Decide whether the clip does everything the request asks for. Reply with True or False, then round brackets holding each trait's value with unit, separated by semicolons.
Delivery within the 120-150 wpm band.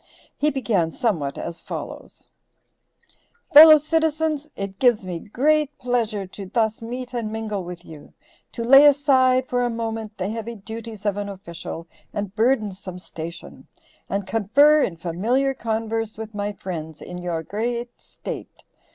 True (145 wpm)